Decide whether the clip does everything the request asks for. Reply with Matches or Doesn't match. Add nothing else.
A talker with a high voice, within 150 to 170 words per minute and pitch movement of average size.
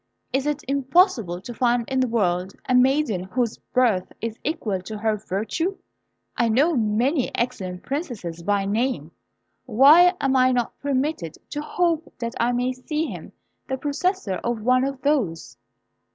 Matches